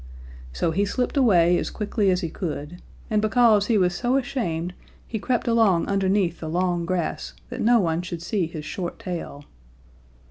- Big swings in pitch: No, average, 4.2 semitones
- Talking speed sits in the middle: Yes, average, 175 wpm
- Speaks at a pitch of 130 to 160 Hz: No, medium, 185 Hz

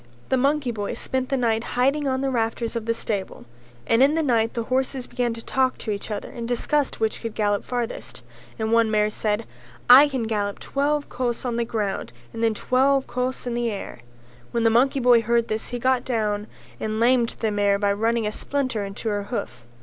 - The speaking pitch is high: Yes, high, 235 Hz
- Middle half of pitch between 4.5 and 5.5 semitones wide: No, average, 3.0 semitones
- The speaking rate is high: Yes, fast, 210 wpm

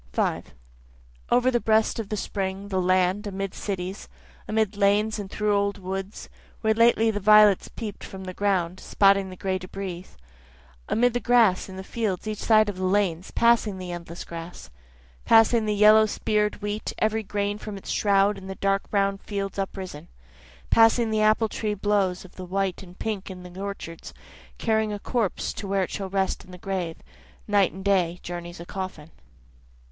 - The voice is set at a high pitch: Yes, high, 200 Hz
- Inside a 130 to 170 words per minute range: No, average, 180 wpm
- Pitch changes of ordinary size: No, narrow, 2.2 semitones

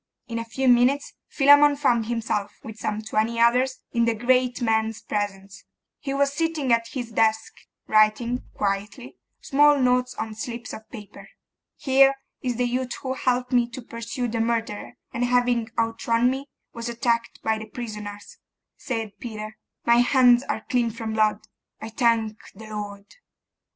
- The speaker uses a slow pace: No, average, 155 wpm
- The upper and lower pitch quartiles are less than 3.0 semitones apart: Yes, narrow, 2.4 semitones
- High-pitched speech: Yes, high, 235 Hz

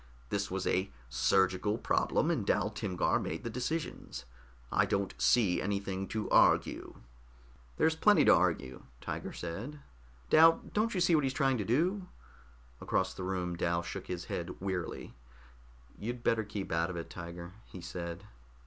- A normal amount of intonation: No, wide, 6.0 semitones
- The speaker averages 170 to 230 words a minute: No, average, 160 wpm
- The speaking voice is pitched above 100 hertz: No, very low, 95 Hz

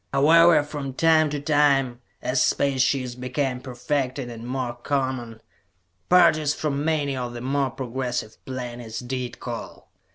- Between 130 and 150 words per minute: Yes, slow, 135 wpm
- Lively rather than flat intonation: No, average, 2.8 semitones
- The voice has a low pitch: Yes, low, 130 Hz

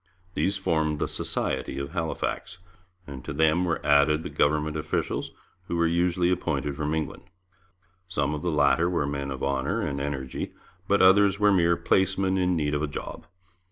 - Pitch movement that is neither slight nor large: Yes, average, 3.6 semitones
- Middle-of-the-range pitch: No, very low, 80 Hz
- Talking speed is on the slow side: No, average, 175 wpm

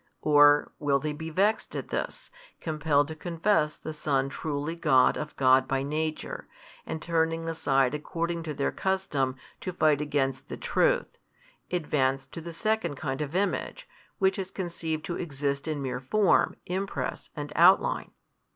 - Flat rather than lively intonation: No, average, 3.4 semitones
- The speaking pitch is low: No, medium, 155 Hz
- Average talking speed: Yes, average, 155 wpm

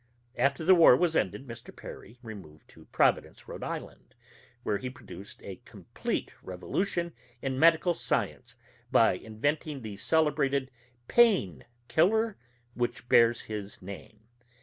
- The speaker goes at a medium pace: No, slow, 125 wpm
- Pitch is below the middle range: Yes, low, 130 Hz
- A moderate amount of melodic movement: No, wide, 7.0 semitones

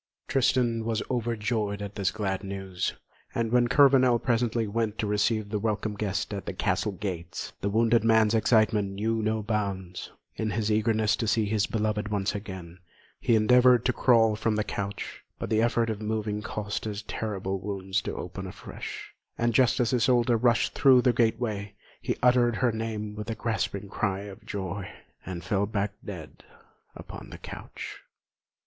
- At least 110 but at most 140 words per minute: No, average, 170 wpm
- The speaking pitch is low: Yes, low, 110 Hz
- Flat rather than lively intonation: Yes, narrow, 2.3 semitones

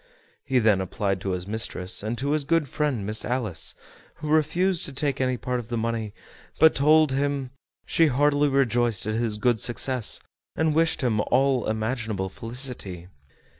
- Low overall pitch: Yes, low, 125 Hz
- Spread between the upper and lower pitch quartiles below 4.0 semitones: No, average, 4.6 semitones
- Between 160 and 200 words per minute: Yes, average, 170 wpm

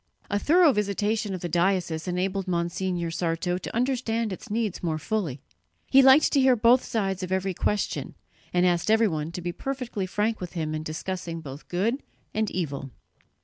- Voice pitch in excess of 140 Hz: Yes, high, 190 Hz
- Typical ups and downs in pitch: Yes, average, 4.4 semitones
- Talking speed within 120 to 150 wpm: No, average, 175 wpm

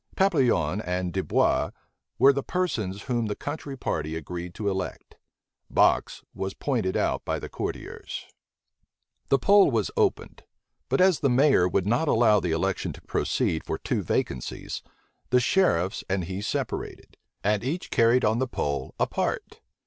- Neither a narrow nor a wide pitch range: No, wide, 7.0 semitones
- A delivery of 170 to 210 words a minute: No, average, 150 wpm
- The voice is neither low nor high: No, low, 110 Hz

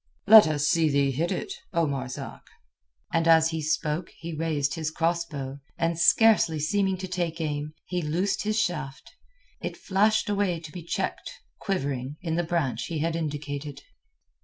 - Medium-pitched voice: Yes, medium, 165 Hz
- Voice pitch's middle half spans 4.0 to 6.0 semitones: No, average, 3.0 semitones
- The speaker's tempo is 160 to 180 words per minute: Yes, average, 165 wpm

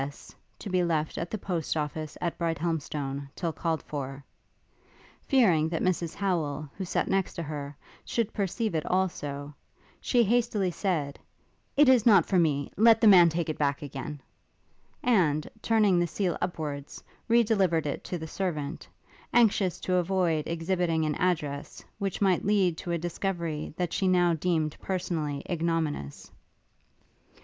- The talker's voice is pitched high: No, medium, 170 Hz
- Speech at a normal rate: Yes, average, 155 wpm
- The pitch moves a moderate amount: Yes, average, 3.8 semitones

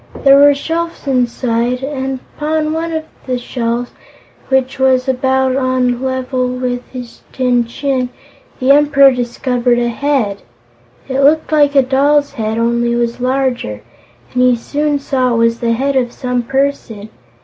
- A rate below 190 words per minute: Yes, average, 160 wpm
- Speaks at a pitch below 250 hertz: No, very high, 255 Hz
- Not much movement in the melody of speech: Yes, narrow, 2.3 semitones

